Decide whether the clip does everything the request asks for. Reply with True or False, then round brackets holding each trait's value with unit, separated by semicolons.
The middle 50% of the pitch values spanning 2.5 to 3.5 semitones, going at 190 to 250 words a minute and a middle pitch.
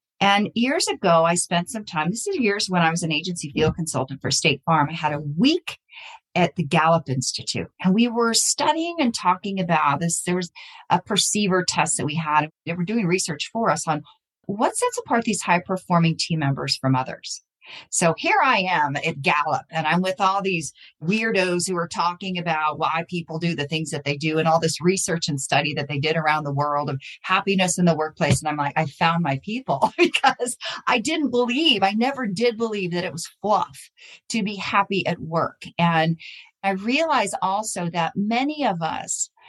False (4.8 semitones; 205 wpm; 175 Hz)